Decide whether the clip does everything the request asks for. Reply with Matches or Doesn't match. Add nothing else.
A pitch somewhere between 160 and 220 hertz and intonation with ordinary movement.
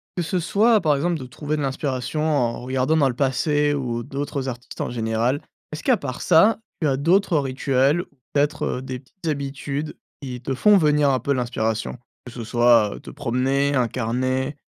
Doesn't match